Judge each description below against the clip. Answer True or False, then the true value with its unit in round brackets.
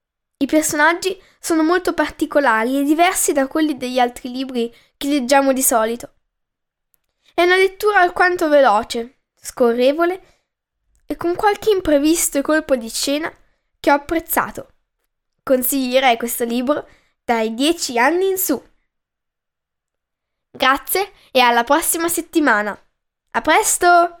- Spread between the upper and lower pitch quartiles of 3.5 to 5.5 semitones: True (4.7 semitones)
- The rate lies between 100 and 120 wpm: True (115 wpm)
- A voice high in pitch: True (295 Hz)